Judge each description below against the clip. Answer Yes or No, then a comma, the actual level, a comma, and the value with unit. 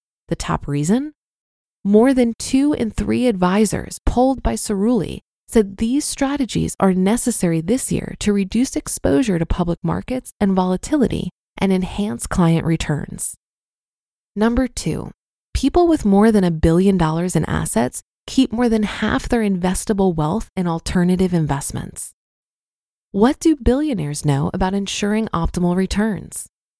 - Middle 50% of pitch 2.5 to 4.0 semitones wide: No, average, 5.0 semitones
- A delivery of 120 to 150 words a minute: Yes, slow, 135 wpm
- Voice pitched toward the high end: Yes, high, 205 Hz